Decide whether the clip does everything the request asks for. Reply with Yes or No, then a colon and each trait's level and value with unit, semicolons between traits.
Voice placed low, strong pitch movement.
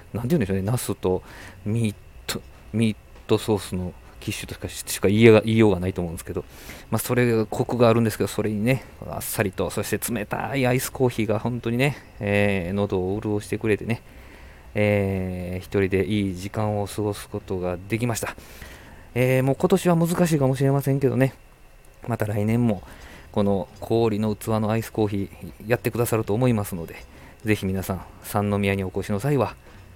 No: low, 105 Hz; average, 3.6 semitones